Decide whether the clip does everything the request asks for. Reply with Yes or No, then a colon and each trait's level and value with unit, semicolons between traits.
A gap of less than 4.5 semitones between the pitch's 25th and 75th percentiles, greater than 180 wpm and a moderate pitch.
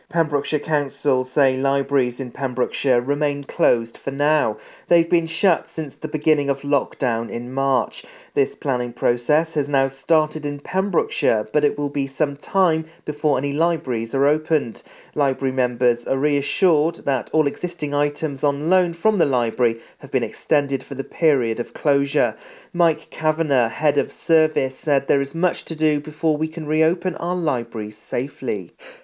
No: average, 3.0 semitones; average, 160 wpm; medium, 145 Hz